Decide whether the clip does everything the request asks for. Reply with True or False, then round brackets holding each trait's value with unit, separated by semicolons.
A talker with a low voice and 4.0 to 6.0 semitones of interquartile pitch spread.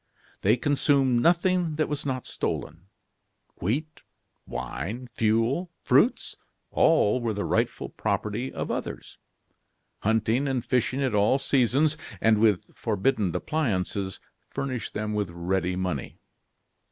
True (115 Hz; 5.2 semitones)